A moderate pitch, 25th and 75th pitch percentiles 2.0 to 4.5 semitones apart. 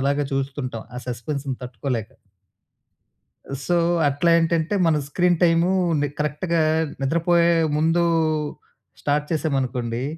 Yes: medium, 150 Hz; average, 4.0 semitones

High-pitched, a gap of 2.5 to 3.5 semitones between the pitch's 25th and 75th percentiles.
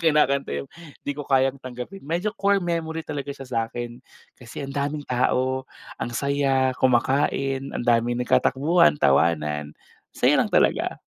No: low, 135 Hz; average, 3.2 semitones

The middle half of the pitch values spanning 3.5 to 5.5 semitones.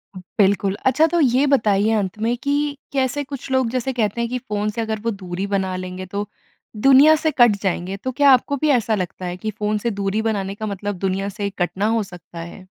Yes: average, 4.6 semitones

